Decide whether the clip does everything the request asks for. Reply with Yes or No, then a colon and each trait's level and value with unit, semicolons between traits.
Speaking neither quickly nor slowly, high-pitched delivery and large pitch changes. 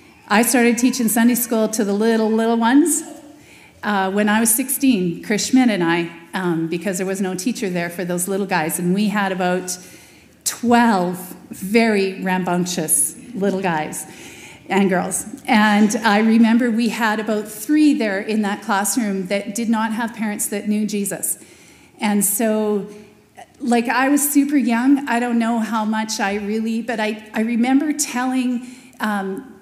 No: average, 160 wpm; high, 215 Hz; average, 3.4 semitones